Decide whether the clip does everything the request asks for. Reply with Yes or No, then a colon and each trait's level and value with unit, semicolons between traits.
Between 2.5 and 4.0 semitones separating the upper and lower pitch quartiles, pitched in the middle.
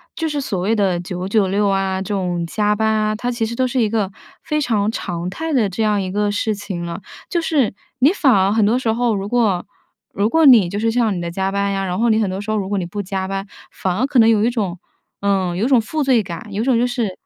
No: average, 3.4 semitones; high, 210 Hz